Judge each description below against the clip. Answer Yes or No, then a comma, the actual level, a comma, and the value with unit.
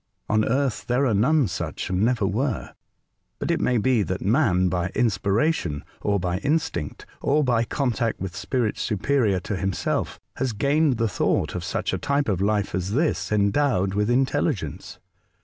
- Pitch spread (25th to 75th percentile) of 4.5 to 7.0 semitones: Yes, wide, 5.6 semitones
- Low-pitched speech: Yes, low, 110 Hz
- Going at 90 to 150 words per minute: No, average, 165 wpm